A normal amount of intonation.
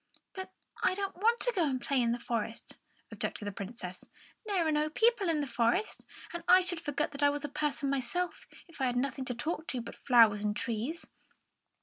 No: wide, 6.3 semitones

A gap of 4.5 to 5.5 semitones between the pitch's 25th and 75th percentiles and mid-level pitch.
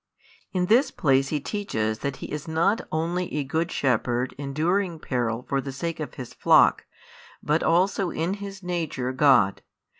Yes: average, 5.1 semitones; medium, 155 Hz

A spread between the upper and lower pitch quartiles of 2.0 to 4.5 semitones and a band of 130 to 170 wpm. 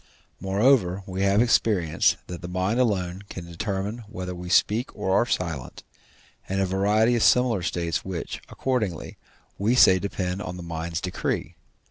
Yes: average, 3.2 semitones; average, 155 wpm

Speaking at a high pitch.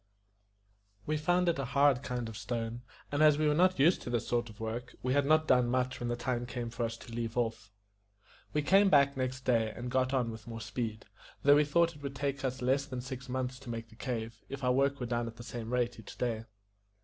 No: low, 125 Hz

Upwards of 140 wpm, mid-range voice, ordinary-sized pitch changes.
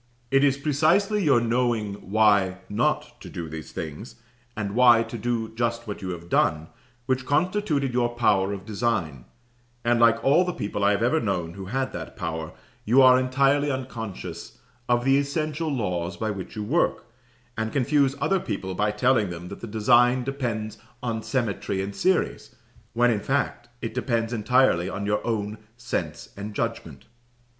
No: average, 170 wpm; low, 115 Hz; average, 4.5 semitones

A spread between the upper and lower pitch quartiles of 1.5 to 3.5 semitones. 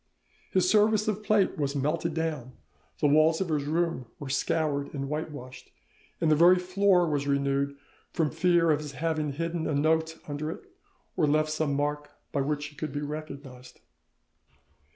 Yes: narrow, 2.6 semitones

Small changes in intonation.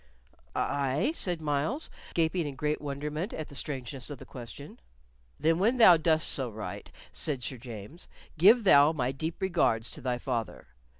No: average, 4.1 semitones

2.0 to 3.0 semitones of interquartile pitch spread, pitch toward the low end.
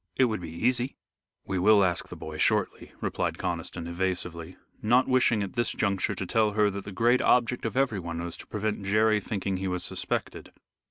No: average, 3.7 semitones; low, 100 Hz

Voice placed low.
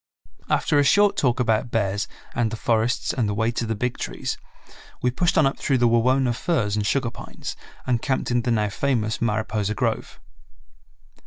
Yes: low, 120 Hz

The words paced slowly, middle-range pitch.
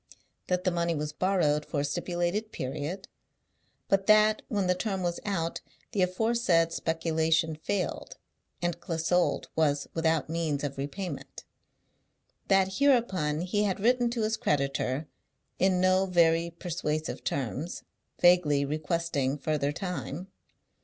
Yes: slow, 125 wpm; medium, 170 Hz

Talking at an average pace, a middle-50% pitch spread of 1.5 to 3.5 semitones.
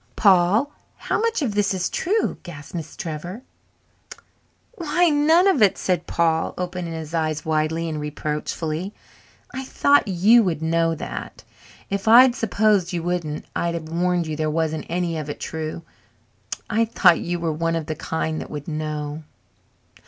No: average, 160 wpm; average, 4.6 semitones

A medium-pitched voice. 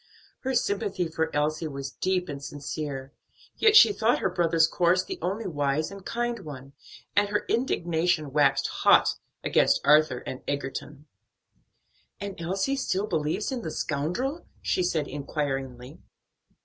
Yes: medium, 160 Hz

